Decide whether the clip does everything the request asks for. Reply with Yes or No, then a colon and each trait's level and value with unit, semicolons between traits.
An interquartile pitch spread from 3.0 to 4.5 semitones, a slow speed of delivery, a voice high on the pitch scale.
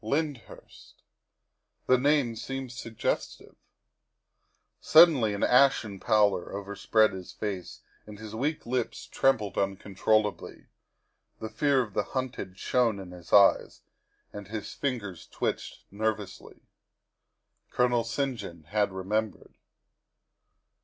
No: average, 3.9 semitones; slow, 105 wpm; low, 110 Hz